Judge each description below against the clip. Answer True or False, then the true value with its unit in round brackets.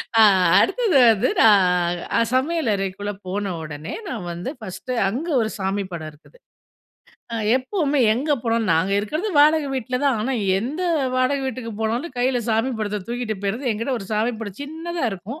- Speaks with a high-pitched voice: True (230 Hz)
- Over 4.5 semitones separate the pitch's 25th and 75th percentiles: True (5.3 semitones)